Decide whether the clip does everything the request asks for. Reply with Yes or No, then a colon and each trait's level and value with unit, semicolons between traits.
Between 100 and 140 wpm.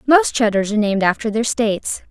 No: average, 200 wpm